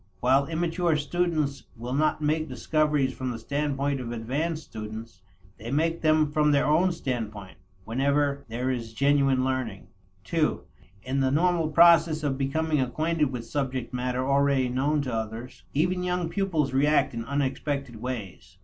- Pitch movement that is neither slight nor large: Yes, average, 3.6 semitones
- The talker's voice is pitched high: No, medium, 140 Hz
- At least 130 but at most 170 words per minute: Yes, average, 150 wpm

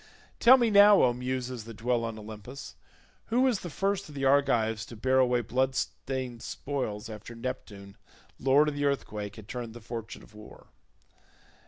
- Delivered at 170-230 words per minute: Yes, average, 175 wpm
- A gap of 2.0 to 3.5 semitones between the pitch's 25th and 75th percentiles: No, average, 3.9 semitones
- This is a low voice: Yes, low, 125 Hz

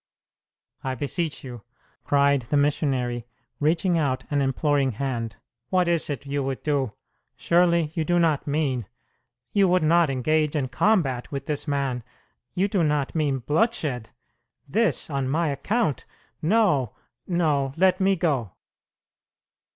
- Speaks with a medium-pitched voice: Yes, medium, 145 Hz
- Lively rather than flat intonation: No, average, 4.1 semitones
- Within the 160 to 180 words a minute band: No, slow, 135 wpm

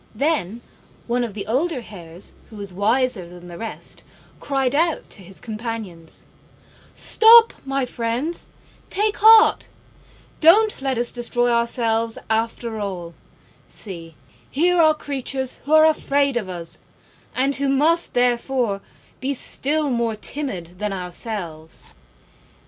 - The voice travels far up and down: Yes, wide, 5.7 semitones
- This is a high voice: Yes, high, 240 Hz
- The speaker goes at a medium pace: No, slow, 125 wpm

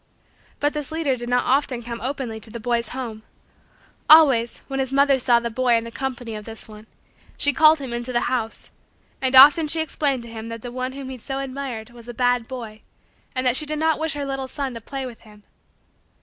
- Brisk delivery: Yes, fast, 225 wpm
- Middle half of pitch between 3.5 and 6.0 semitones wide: No, average, 2.9 semitones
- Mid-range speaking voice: No, very high, 255 Hz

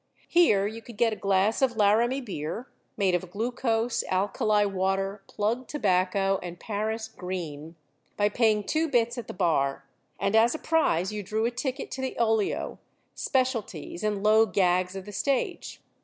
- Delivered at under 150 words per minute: No, average, 165 wpm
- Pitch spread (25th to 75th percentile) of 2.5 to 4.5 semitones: Yes, average, 3.7 semitones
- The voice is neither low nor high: No, high, 210 Hz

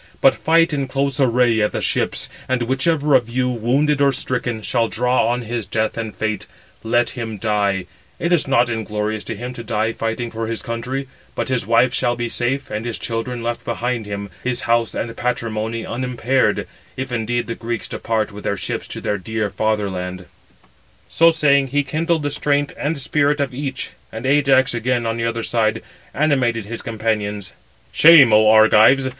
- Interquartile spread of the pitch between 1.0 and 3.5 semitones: Yes, average, 3.1 semitones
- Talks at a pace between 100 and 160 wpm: No, average, 185 wpm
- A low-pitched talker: Yes, low, 120 Hz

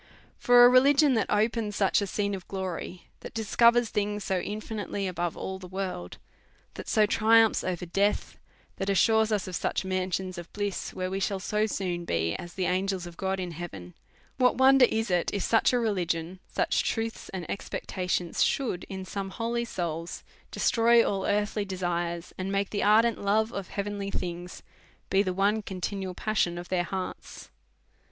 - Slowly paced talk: No, average, 175 wpm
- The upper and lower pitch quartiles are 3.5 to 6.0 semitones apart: No, average, 3.1 semitones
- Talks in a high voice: Yes, high, 195 Hz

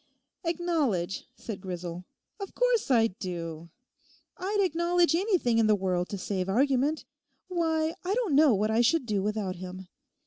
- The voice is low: No, high, 235 Hz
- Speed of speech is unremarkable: Yes, average, 150 wpm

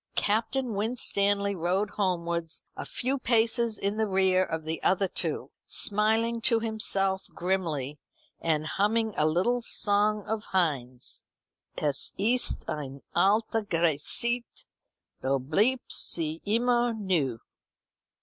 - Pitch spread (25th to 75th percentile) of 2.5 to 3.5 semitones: No, average, 5.0 semitones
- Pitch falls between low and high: No, high, 200 Hz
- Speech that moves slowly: Yes, slow, 115 wpm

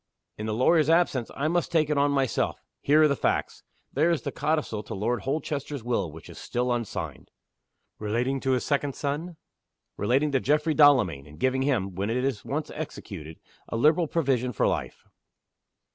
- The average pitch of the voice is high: No, low, 135 Hz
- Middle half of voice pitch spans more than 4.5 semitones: Yes, average, 4.9 semitones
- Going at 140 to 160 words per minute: No, average, 180 wpm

